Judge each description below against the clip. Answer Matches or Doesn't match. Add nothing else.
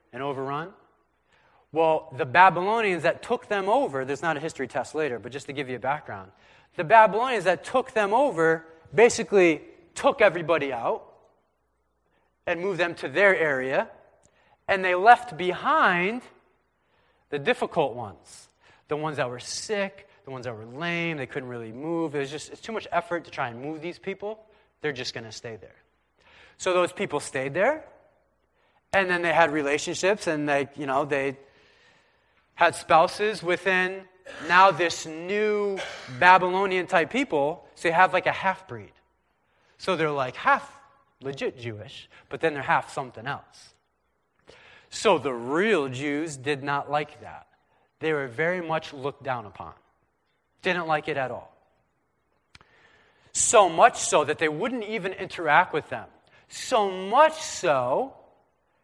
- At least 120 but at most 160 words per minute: Matches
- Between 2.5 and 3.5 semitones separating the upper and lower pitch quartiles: Doesn't match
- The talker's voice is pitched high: Doesn't match